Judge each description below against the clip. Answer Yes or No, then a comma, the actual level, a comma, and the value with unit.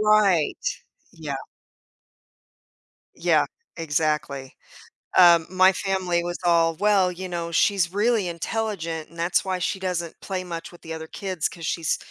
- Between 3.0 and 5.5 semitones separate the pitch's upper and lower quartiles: No, narrow, 2.4 semitones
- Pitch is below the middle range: No, medium, 175 Hz